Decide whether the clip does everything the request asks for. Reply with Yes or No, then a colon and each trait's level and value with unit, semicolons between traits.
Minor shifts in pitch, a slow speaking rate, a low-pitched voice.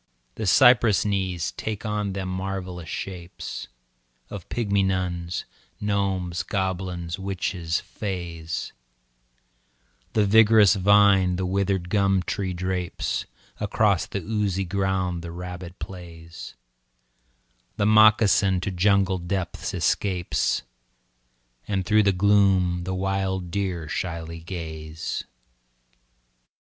Yes: narrow, 2.1 semitones; slow, 100 wpm; very low, 95 Hz